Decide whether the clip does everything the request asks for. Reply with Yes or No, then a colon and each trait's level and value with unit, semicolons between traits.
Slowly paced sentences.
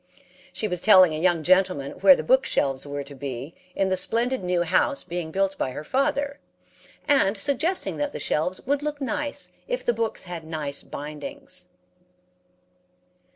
No: average, 165 wpm